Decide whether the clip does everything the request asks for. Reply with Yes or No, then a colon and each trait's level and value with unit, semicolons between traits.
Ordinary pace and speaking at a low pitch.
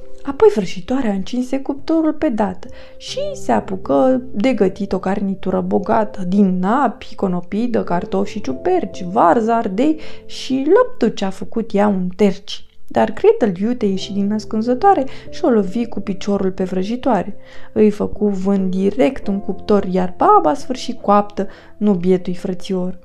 No: average, 145 wpm; high, 210 Hz